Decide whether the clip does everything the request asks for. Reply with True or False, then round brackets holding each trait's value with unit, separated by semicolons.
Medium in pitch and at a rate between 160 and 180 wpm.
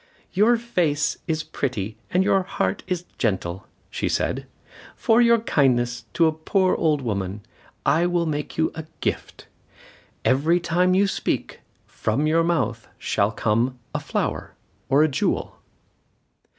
False (155 Hz; 140 wpm)